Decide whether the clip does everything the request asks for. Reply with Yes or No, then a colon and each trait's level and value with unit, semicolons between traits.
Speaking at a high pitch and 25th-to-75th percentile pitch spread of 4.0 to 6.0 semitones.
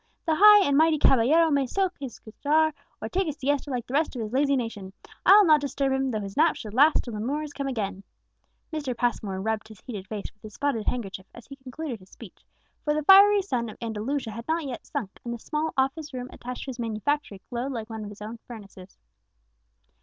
Yes: very high, 255 Hz; average, 5.2 semitones